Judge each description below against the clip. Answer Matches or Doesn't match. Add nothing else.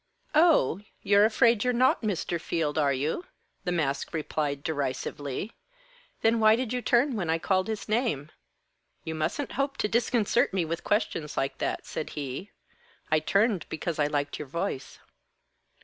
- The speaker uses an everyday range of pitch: Doesn't match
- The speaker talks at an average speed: Matches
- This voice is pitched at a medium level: Matches